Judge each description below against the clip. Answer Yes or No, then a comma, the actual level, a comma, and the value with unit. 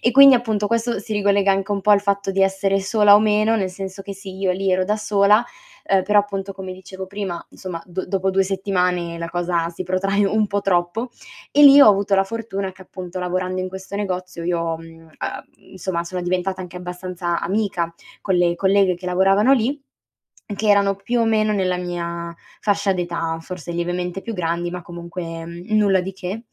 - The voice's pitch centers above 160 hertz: Yes, high, 190 Hz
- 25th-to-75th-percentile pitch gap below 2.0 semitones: No, narrow, 2.3 semitones